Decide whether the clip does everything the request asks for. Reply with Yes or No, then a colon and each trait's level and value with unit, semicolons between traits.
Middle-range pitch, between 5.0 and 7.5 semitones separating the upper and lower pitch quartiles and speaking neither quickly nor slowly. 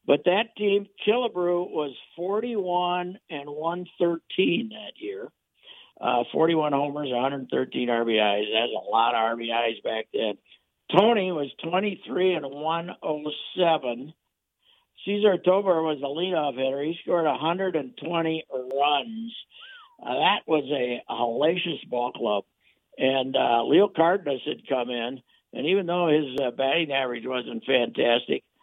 No: medium, 160 Hz; wide, 5.5 semitones; slow, 130 wpm